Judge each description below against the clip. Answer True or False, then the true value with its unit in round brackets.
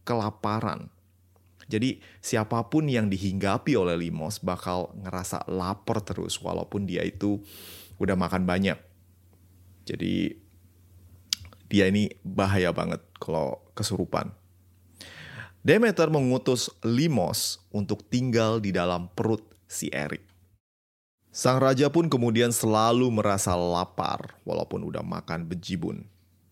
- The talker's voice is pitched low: True (95 Hz)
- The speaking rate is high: False (100 wpm)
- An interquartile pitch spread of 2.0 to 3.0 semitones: False (3.6 semitones)